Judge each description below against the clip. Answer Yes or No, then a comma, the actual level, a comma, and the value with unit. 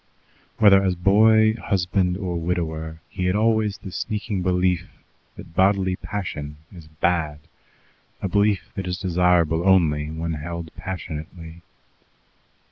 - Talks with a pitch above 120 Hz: No, very low, 90 Hz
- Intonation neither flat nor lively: Yes, average, 3.1 semitones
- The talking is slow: Yes, slow, 125 wpm